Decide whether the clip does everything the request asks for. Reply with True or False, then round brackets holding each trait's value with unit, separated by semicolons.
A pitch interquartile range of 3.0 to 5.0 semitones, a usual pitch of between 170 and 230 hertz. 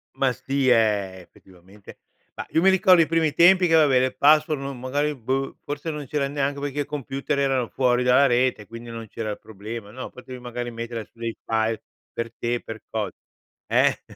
False (3.8 semitones; 130 Hz)